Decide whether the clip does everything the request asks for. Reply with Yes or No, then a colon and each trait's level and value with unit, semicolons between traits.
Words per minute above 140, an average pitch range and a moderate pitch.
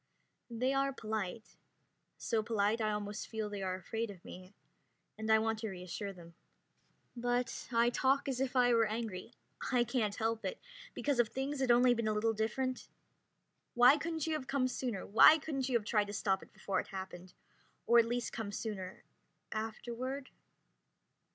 No: average, 175 wpm; average, 3.3 semitones; high, 225 Hz